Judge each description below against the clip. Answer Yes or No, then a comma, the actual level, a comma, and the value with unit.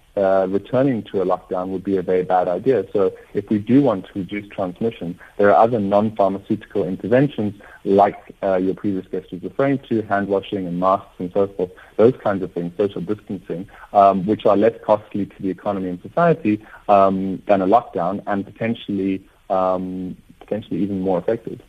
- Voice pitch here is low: Yes, low, 100 Hz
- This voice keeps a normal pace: Yes, average, 185 wpm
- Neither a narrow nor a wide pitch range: No, narrow, 2.0 semitones